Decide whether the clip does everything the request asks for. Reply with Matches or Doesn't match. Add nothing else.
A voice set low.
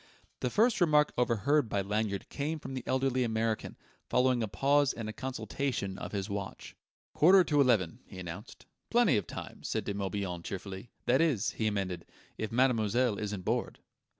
Matches